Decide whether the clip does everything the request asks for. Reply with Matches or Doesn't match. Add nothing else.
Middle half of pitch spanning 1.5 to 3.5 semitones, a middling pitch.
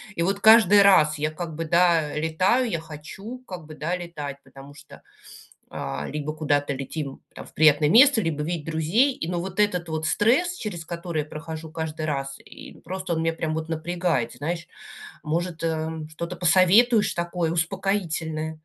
Matches